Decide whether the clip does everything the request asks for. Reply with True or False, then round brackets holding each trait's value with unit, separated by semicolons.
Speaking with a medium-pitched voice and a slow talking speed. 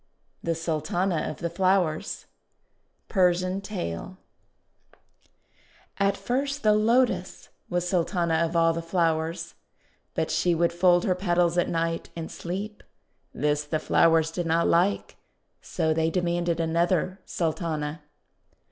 True (170 Hz; 120 wpm)